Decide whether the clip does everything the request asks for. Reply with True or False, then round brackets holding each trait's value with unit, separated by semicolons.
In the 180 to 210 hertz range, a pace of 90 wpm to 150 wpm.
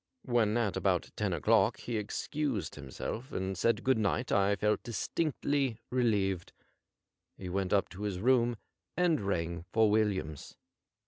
False (105 Hz; 140 wpm)